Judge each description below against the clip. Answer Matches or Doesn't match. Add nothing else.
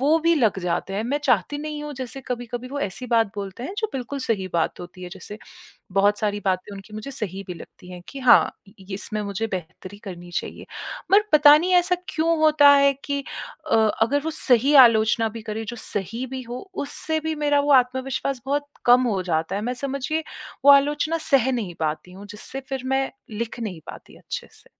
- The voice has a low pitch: Doesn't match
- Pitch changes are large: Matches